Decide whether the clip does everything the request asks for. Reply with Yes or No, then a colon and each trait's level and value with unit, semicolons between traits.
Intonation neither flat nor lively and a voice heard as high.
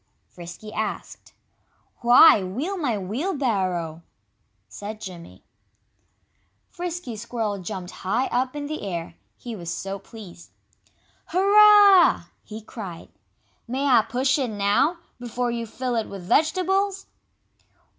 No: wide, 6.8 semitones; high, 230 Hz